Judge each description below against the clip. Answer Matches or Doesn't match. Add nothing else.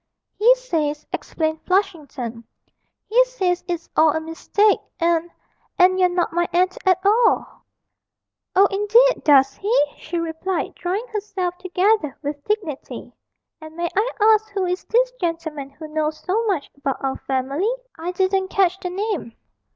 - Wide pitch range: Doesn't match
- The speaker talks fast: Doesn't match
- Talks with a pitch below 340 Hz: Doesn't match